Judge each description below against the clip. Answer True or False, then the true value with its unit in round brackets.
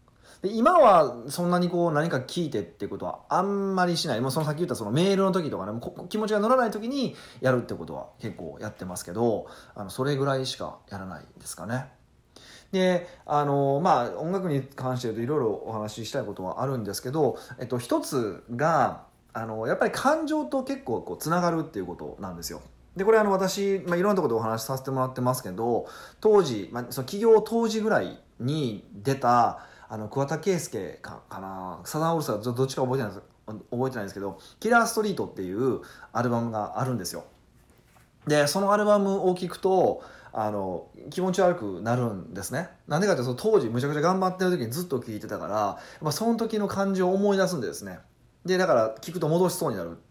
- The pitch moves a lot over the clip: True (8.6 semitones)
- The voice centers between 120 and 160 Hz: True (140 Hz)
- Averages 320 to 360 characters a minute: False (415 characters per minute)